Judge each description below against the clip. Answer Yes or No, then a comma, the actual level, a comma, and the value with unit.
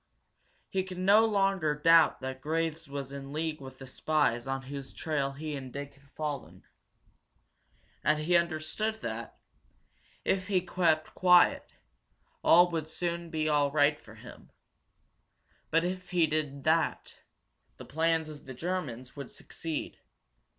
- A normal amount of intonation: Yes, average, 3.4 semitones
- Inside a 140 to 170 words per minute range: Yes, average, 145 wpm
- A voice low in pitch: No, medium, 155 Hz